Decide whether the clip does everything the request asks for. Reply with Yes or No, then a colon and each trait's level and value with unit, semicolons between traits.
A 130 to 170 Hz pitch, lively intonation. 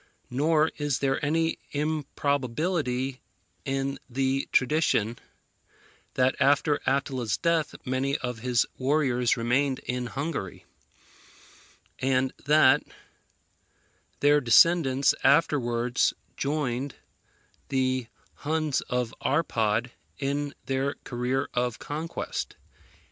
No: low, 135 Hz; average, 2.8 semitones